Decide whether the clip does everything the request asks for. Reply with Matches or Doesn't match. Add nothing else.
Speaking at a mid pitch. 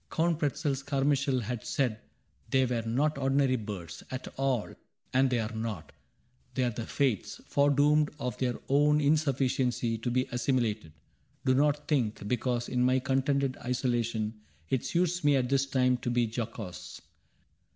Doesn't match